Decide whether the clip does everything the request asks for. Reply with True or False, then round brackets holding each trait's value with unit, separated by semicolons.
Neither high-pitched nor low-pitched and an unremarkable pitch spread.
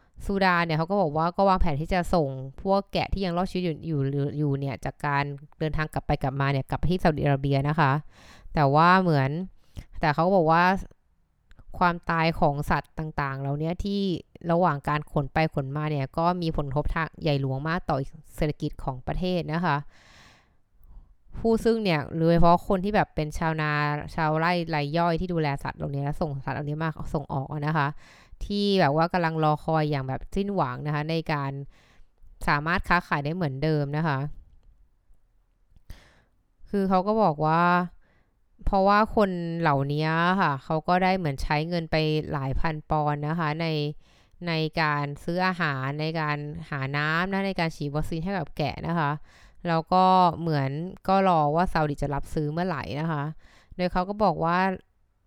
True (155 Hz; 3.4 semitones)